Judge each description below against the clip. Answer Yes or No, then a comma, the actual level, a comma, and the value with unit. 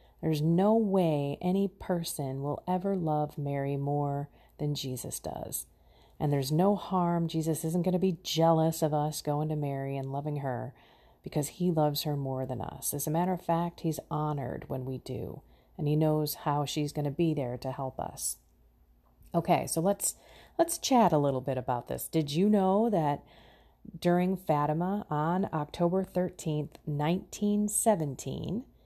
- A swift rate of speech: No, average, 165 wpm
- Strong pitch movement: No, average, 3.9 semitones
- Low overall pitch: No, medium, 155 Hz